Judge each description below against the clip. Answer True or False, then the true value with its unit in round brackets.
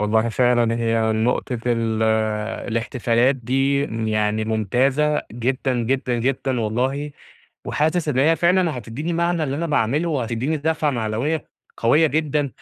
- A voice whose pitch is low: True (130 Hz)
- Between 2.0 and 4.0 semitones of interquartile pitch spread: False (4.6 semitones)